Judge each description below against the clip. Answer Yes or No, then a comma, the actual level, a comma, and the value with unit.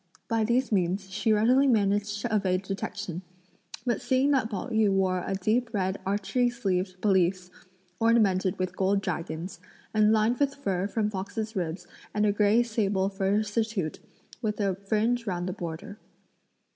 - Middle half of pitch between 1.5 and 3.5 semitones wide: Yes, average, 2.9 semitones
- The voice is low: No, high, 205 Hz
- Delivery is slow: No, average, 160 wpm